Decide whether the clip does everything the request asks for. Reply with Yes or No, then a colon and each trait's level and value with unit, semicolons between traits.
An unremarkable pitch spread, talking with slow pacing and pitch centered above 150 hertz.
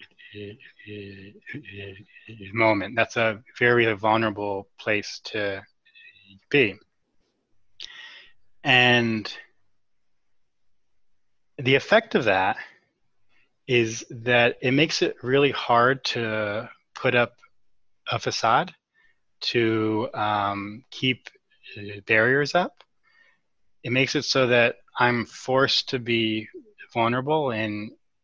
No: average, 3.8 semitones; slow, 85 wpm; low, 120 Hz